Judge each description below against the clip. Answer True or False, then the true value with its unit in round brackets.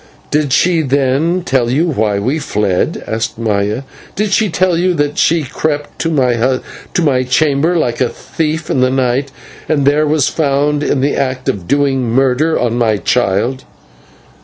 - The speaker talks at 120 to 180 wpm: True (160 wpm)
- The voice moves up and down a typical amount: True (3.9 semitones)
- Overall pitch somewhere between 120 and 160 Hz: True (135 Hz)